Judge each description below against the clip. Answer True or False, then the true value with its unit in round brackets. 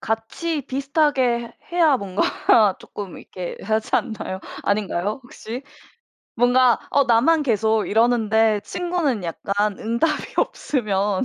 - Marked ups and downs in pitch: False (4.5 semitones)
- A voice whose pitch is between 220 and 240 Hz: True (230 Hz)